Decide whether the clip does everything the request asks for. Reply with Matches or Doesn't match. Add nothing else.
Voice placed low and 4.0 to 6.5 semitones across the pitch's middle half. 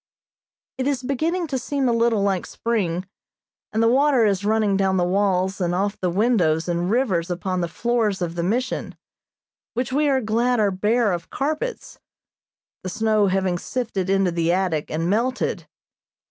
Doesn't match